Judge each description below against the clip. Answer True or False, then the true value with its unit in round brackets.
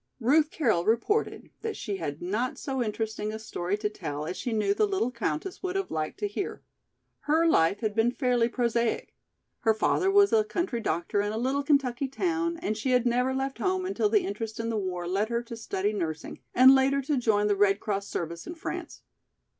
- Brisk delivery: True (210 wpm)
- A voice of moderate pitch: False (235 Hz)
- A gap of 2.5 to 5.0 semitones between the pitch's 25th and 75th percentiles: False (5.4 semitones)